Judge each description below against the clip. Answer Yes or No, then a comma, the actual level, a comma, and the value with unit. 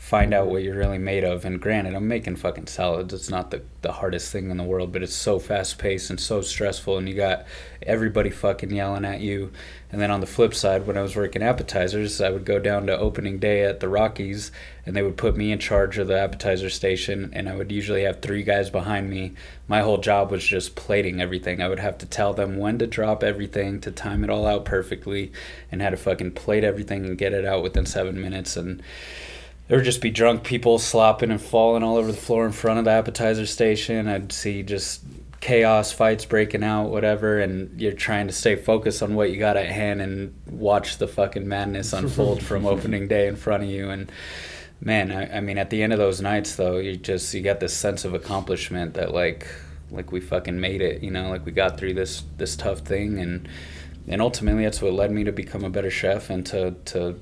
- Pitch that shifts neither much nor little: No, narrow, 2.1 semitones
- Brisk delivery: Yes, fast, 230 wpm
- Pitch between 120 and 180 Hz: No, low, 100 Hz